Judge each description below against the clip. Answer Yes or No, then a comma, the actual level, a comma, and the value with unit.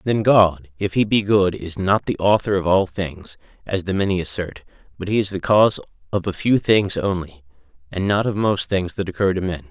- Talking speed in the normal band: No, fast, 225 wpm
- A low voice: Yes, very low, 95 Hz